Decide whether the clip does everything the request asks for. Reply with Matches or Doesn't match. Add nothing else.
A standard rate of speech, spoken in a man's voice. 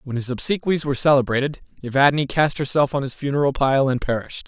Matches